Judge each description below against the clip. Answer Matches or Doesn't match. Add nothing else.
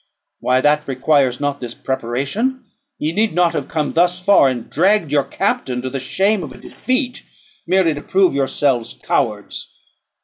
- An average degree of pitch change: Doesn't match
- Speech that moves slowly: Doesn't match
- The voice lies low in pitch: Doesn't match